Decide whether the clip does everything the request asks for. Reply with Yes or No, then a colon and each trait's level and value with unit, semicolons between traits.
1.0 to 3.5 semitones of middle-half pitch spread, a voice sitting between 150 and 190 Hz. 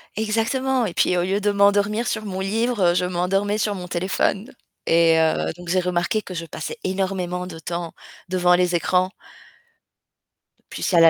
Yes: average, 2.8 semitones; medium, 185 Hz